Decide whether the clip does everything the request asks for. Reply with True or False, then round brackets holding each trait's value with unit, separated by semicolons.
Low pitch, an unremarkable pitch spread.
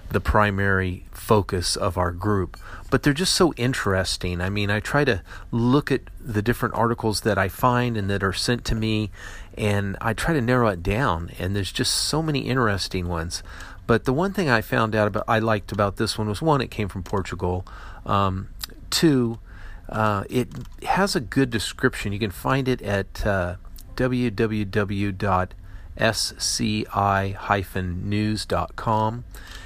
True (105 Hz; 3.8 semitones)